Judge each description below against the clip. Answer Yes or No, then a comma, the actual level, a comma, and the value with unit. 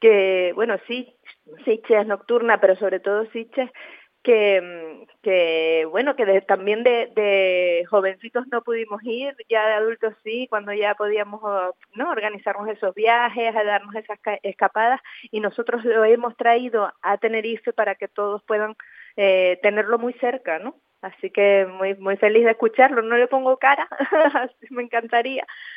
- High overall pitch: Yes, high, 215 Hz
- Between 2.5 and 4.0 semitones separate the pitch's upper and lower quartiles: Yes, average, 2.9 semitones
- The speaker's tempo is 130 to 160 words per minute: Yes, average, 155 wpm